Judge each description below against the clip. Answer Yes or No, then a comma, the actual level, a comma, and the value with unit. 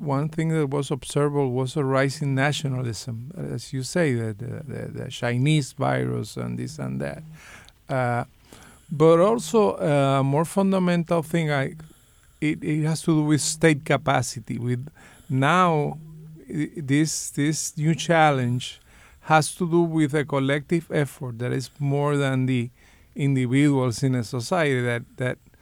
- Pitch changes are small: No, average, 3.9 semitones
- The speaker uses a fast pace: No, average, 145 wpm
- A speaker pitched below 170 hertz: Yes, medium, 140 Hz